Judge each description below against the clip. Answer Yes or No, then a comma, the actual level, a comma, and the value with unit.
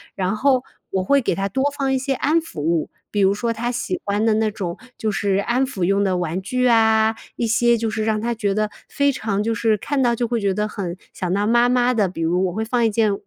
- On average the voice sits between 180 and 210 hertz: No, high, 220 Hz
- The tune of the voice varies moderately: Yes, average, 3.5 semitones